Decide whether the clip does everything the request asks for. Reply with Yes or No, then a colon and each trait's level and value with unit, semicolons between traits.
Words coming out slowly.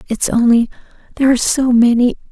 Yes: slow, 130 wpm